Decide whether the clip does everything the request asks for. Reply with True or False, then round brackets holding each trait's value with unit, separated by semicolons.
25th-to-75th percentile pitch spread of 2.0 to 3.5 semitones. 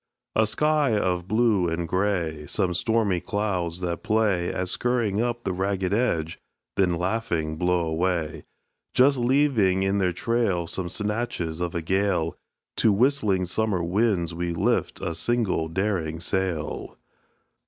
False (4.3 semitones)